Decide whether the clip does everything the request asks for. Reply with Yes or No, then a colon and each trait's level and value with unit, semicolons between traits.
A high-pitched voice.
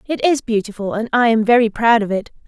Yes: high, 225 Hz